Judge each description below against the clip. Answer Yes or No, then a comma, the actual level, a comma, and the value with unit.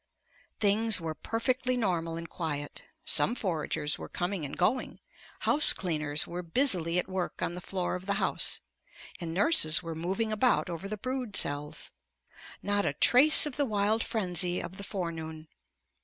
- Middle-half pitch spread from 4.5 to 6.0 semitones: Yes, average, 4.9 semitones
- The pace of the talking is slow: No, average, 160 wpm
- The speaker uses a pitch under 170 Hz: No, medium, 185 Hz